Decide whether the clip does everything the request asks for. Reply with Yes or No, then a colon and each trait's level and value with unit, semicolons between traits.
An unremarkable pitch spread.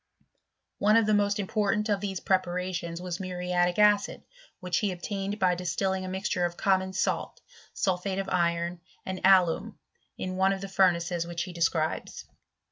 No: narrow, 1.9 semitones